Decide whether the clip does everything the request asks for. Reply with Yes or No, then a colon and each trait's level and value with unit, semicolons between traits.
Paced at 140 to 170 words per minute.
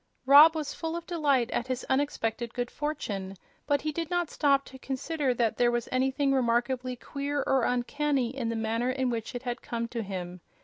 No: average, 195 wpm